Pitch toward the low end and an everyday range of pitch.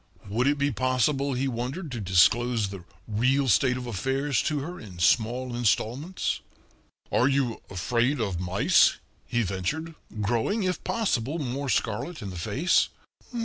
Yes: low, 125 Hz; average, 4.4 semitones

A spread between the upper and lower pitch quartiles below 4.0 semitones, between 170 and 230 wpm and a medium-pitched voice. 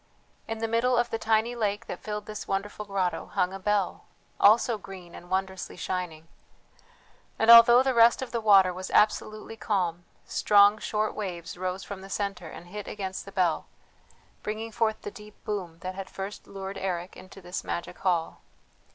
No: average, 2.7 semitones; average, 175 wpm; high, 200 Hz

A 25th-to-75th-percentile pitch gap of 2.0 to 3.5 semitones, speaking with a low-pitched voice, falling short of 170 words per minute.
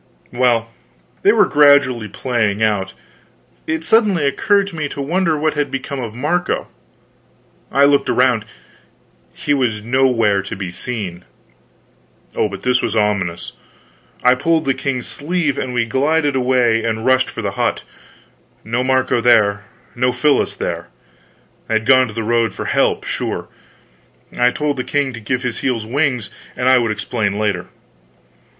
No: average, 4.1 semitones; low, 125 Hz; average, 160 wpm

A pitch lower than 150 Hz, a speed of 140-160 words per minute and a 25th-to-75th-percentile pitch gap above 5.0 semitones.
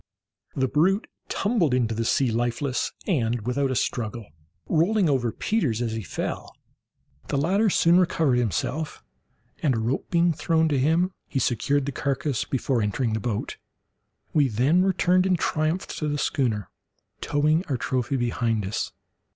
Yes: medium, 140 Hz; average, 150 wpm; wide, 5.4 semitones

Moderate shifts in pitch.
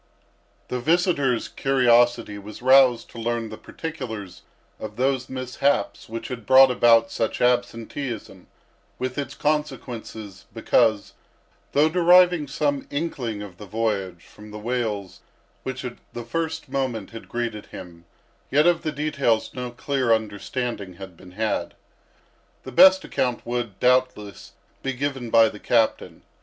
Yes: average, 3.8 semitones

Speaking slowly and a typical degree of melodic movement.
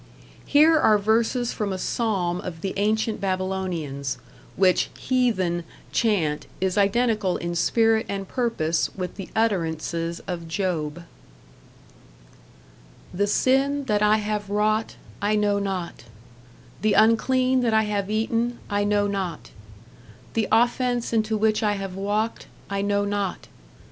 Yes: slow, 130 wpm; average, 3.1 semitones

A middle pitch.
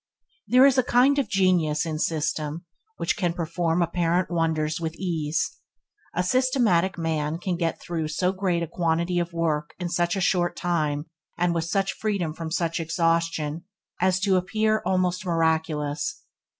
Yes: medium, 170 Hz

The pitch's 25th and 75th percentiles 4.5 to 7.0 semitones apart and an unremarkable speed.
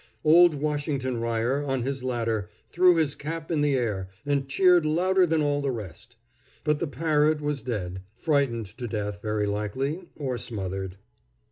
Yes: average, 5.2 semitones; average, 160 wpm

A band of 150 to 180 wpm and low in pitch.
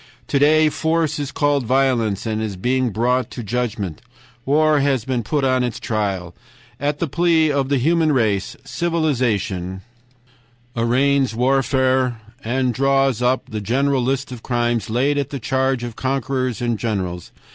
Yes: average, 155 wpm; low, 130 Hz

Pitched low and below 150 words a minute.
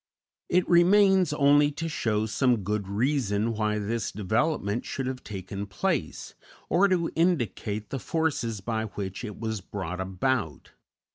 Yes: low, 115 Hz; average, 140 wpm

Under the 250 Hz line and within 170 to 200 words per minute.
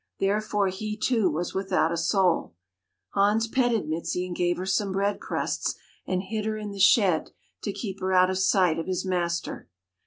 Yes: high, 190 Hz; average, 185 wpm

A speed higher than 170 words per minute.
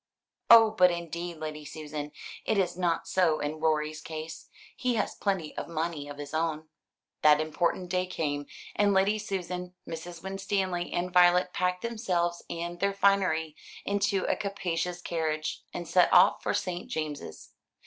No: average, 155 wpm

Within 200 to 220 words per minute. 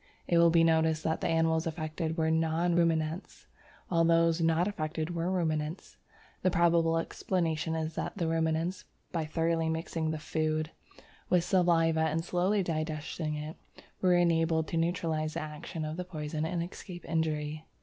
No: average, 160 wpm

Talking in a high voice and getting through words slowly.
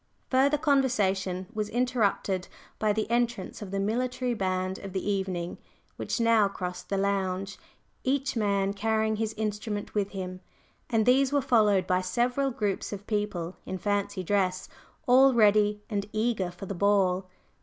No: high, 205 Hz; average, 155 wpm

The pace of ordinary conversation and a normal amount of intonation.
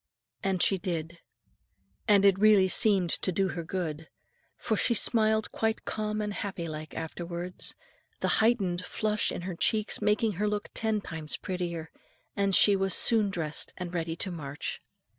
Yes: average, 160 wpm; average, 3.6 semitones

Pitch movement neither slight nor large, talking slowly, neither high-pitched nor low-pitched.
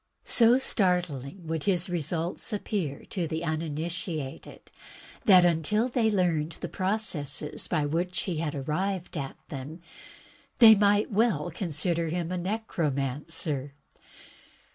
Yes: average, 4.3 semitones; slow, 120 wpm; medium, 170 Hz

